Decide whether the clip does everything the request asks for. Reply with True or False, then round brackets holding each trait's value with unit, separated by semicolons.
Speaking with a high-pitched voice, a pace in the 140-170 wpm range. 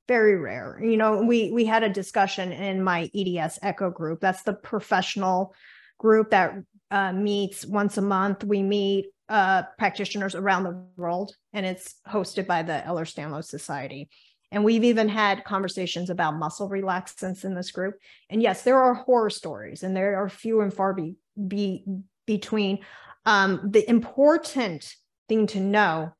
True (195 Hz; 165 wpm)